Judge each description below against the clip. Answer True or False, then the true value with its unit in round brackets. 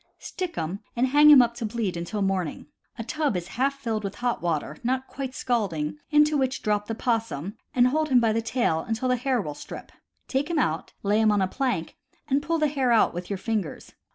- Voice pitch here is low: False (230 Hz)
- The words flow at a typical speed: False (225 wpm)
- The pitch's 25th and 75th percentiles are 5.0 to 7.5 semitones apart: True (5.3 semitones)